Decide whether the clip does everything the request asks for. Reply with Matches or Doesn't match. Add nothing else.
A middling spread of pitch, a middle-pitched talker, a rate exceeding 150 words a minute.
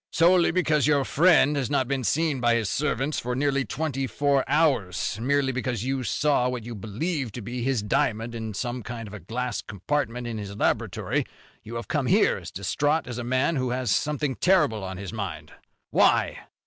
Doesn't match